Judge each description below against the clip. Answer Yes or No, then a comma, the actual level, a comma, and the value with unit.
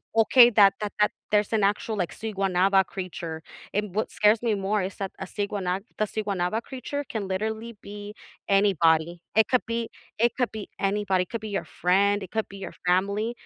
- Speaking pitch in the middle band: No, high, 205 Hz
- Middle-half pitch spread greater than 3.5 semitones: No, narrow, 2.4 semitones